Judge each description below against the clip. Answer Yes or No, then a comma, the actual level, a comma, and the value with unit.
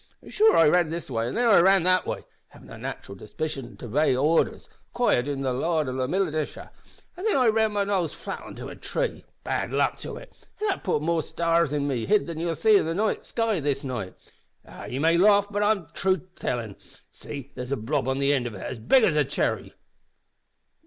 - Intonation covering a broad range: Yes, wide, 6.8 semitones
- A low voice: No, medium, 160 Hz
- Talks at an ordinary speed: No, fast, 220 wpm